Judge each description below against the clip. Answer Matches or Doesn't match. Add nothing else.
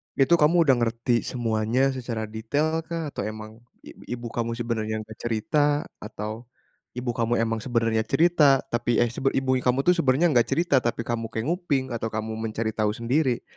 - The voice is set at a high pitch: Doesn't match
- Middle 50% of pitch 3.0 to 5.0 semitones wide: Matches